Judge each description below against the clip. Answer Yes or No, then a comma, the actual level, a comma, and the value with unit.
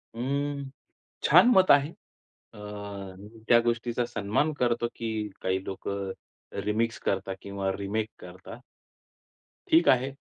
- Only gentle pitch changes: No, average, 4.9 semitones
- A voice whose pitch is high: No, low, 115 Hz